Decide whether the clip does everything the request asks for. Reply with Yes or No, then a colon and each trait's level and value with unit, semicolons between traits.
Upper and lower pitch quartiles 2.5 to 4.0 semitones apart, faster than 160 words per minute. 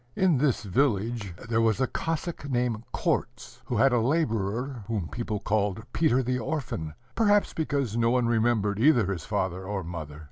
No: average, 4.6 semitones; average, 170 wpm